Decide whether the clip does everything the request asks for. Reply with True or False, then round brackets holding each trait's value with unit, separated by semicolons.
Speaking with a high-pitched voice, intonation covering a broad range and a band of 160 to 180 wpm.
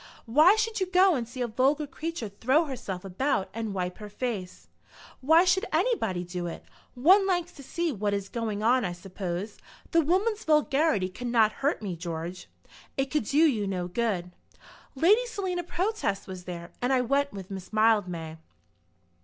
True (235 Hz; 8.8 semitones; 175 wpm)